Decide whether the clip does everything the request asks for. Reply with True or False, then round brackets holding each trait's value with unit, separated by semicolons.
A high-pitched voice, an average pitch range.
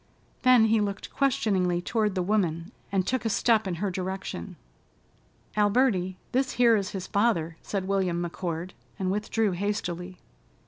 True (195 Hz; 3.4 semitones)